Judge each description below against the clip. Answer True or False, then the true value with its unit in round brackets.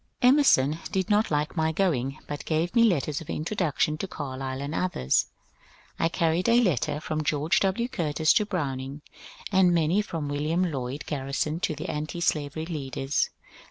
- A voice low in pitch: False (155 Hz)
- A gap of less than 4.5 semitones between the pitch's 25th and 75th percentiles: True (3.9 semitones)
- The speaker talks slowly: False (160 wpm)